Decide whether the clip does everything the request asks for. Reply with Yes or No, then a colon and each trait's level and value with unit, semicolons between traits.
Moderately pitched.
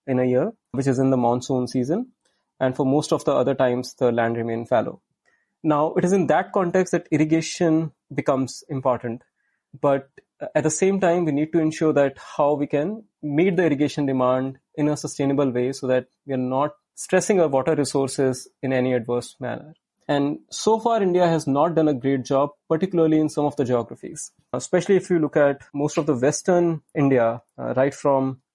Yes: medium, 145 Hz